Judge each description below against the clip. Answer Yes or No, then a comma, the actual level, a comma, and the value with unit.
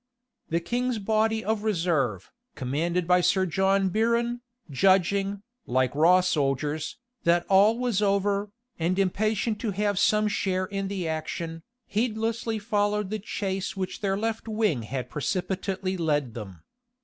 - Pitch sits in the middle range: No, high, 195 Hz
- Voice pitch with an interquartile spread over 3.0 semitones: Yes, average, 4.1 semitones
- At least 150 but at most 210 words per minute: No, slow, 135 wpm